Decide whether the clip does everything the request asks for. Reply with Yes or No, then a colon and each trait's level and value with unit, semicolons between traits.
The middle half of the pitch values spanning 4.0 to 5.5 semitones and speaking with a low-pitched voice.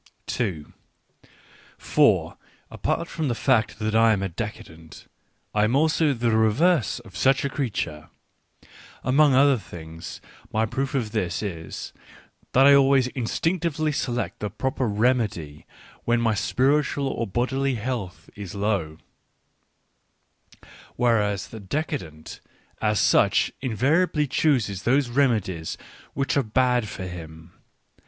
Yes: average, 5.2 semitones; low, 115 Hz